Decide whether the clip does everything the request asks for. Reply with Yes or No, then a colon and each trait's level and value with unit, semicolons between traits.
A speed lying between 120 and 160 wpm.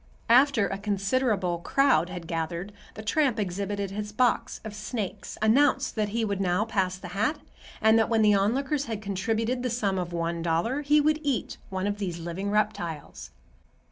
No: average, 175 wpm